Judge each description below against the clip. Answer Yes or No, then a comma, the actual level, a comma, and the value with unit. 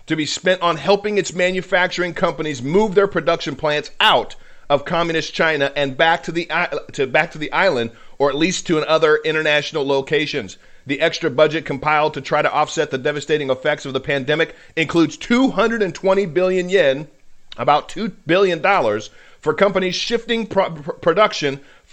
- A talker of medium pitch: Yes, medium, 160 Hz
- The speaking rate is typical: Yes, average, 160 wpm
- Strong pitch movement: No, average, 3.7 semitones